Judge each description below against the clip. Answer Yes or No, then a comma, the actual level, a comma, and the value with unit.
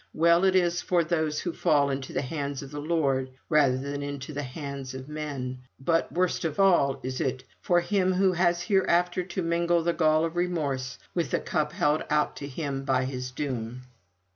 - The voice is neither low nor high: Yes, medium, 150 Hz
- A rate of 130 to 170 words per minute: No, average, 195 wpm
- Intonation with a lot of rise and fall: No, average, 4.1 semitones